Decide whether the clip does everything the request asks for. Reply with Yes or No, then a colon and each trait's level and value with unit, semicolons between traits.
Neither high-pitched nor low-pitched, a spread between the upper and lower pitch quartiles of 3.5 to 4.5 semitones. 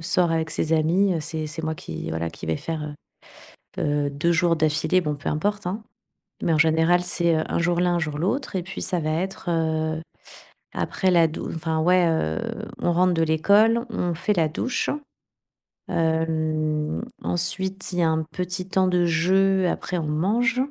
No: medium, 165 Hz; narrow, 2.4 semitones